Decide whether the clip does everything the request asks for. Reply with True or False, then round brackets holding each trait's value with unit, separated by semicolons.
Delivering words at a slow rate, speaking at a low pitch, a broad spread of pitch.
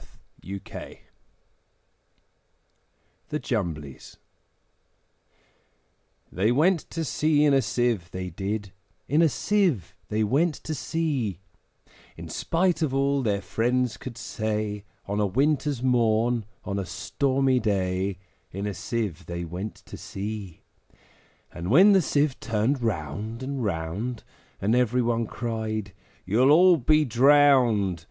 True (125 wpm; 115 Hz; 5.7 semitones)